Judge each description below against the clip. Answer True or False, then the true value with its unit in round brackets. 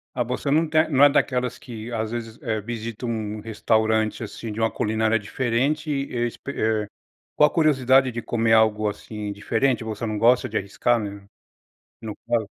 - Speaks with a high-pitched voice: False (115 Hz)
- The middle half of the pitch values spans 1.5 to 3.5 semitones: True (2.7 semitones)